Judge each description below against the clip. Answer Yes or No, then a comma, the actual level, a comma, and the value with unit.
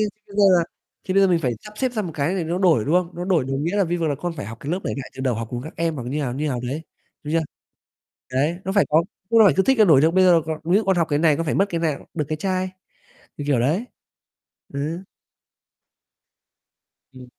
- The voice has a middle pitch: Yes, medium, 165 Hz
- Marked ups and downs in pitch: No, average, 4.6 semitones